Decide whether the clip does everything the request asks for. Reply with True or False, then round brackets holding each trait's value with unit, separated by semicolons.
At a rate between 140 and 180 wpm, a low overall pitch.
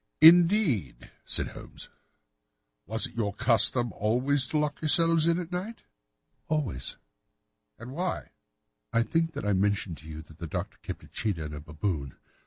True (160 wpm; 115 Hz)